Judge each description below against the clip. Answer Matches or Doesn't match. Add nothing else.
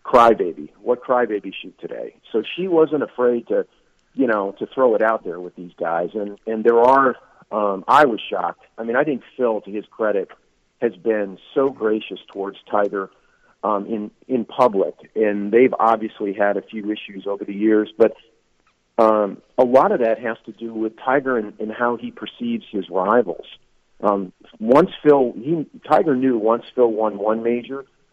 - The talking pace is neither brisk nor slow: Matches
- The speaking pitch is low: Matches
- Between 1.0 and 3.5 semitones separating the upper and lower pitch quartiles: Matches